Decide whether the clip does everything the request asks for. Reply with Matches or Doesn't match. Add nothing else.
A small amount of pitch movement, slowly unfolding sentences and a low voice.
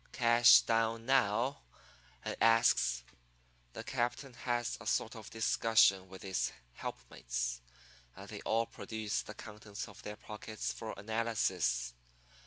Matches